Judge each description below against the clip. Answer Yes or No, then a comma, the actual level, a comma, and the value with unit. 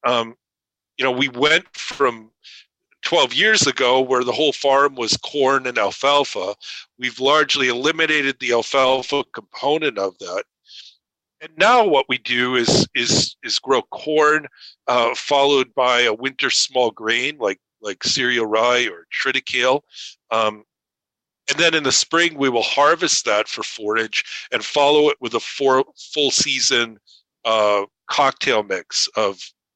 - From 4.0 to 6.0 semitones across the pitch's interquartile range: No, average, 3.3 semitones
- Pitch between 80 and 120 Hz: No, low, 130 Hz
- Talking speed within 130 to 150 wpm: Yes, average, 145 wpm